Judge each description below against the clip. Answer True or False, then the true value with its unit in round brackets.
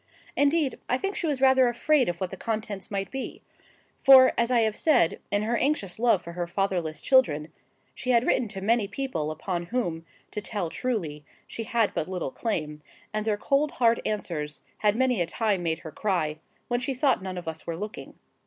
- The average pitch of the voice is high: True (210 Hz)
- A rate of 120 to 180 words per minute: False (200 wpm)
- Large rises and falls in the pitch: True (6.3 semitones)